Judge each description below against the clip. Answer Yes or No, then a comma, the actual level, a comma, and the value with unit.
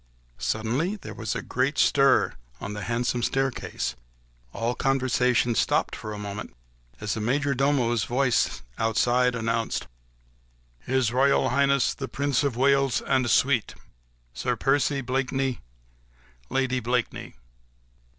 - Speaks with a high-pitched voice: No, low, 125 Hz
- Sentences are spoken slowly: Yes, slow, 120 wpm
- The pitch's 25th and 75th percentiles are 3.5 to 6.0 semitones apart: No, average, 2.9 semitones